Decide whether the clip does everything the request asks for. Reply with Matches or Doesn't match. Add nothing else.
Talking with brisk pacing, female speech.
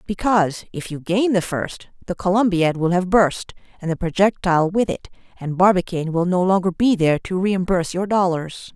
Doesn't match